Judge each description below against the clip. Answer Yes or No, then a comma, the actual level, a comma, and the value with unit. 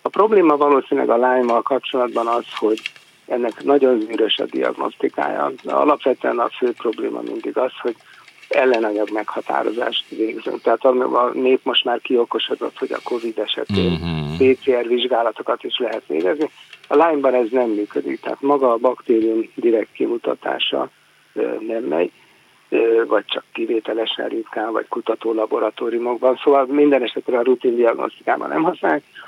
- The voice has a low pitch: Yes, low, 125 Hz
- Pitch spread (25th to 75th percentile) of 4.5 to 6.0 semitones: No, average, 4.1 semitones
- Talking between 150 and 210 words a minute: No, average, 135 wpm